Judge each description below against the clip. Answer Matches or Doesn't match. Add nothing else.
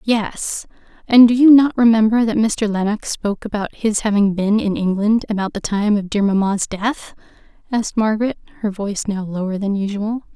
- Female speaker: Matches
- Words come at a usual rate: Matches